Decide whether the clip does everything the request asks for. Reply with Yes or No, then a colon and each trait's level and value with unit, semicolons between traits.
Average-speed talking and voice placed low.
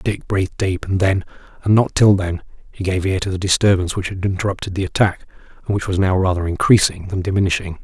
No: fast, 215 wpm; very low, 95 Hz